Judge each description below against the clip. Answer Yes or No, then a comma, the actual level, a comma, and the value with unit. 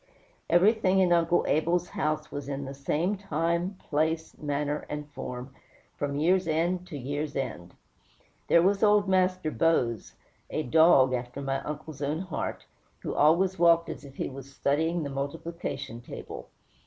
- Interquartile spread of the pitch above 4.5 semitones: No, average, 3.8 semitones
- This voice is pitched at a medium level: Yes, medium, 155 Hz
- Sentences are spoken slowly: No, average, 155 wpm